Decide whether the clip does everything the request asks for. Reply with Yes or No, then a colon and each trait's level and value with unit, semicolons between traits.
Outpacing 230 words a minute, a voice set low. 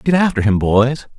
No: average, 200 wpm; low, 130 Hz